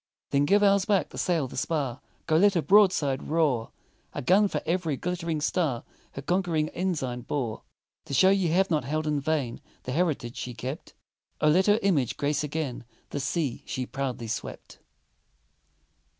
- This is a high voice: No, medium, 155 Hz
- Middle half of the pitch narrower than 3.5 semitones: No, average, 5.1 semitones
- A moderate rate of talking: Yes, average, 170 wpm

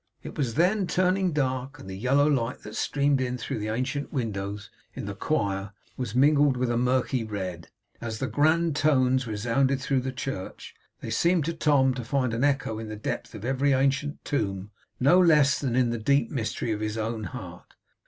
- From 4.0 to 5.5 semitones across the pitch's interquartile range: Yes, average, 4.3 semitones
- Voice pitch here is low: Yes, low, 130 Hz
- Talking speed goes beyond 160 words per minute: Yes, average, 195 wpm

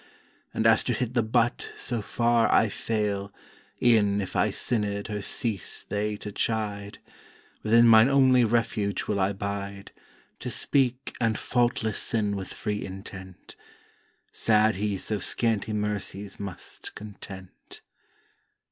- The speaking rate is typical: No, slow, 130 wpm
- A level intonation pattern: Yes, narrow, 2.3 semitones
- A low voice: Yes, low, 105 Hz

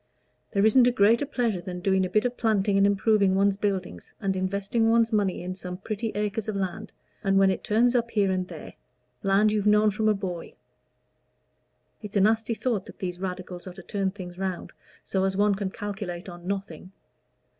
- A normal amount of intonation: No, narrow, 2.3 semitones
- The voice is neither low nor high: No, high, 200 Hz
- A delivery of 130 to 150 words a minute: No, average, 200 wpm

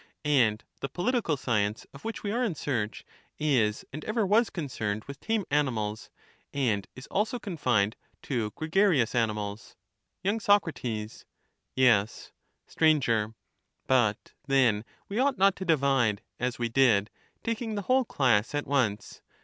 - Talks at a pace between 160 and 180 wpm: No, average, 140 wpm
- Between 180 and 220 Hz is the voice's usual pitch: No, low, 135 Hz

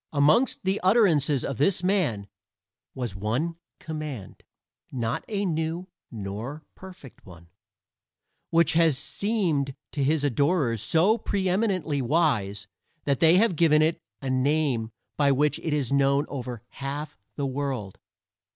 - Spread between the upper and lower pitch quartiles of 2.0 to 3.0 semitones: No, average, 4.6 semitones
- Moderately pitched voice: Yes, medium, 145 Hz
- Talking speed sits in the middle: No, slow, 130 wpm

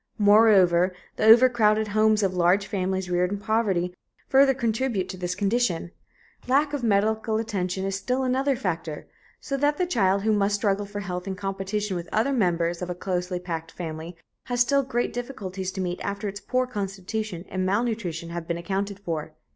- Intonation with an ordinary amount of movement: Yes, average, 3.8 semitones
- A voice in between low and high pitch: No, high, 200 Hz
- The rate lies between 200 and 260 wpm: No, average, 180 wpm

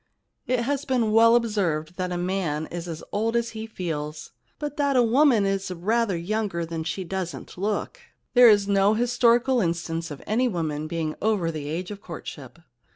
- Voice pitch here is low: No, high, 195 Hz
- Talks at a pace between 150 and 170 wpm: No, average, 180 wpm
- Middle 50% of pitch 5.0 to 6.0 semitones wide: Yes, wide, 5.6 semitones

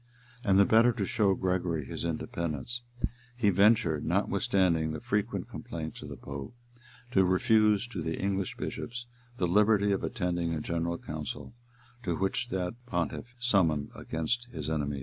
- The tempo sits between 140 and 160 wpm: Yes, average, 155 wpm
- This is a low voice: Yes, very low, 95 Hz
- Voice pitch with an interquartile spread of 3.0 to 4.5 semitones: No, average, 5.0 semitones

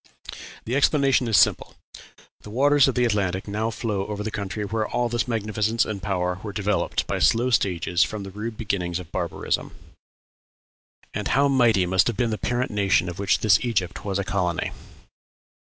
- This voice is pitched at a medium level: No, low, 105 Hz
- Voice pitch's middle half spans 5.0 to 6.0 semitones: No, average, 3.4 semitones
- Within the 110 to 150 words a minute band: No, average, 180 wpm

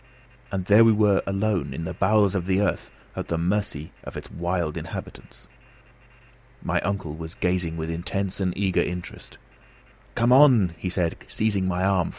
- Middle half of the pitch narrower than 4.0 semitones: Yes, average, 2.9 semitones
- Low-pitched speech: Yes, very low, 95 Hz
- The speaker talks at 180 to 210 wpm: No, average, 165 wpm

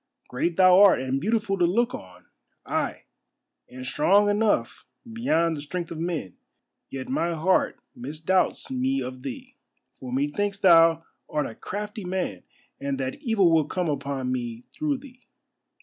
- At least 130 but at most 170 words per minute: Yes, average, 150 wpm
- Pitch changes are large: Yes, wide, 6.8 semitones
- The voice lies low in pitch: No, medium, 170 Hz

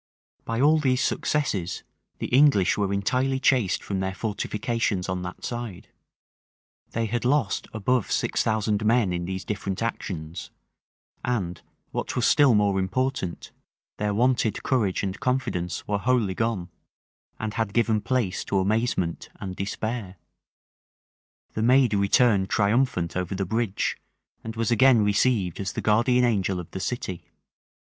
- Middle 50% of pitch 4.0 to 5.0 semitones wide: Yes, average, 4.3 semitones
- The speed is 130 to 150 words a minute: Yes, average, 140 wpm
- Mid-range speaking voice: No, low, 105 Hz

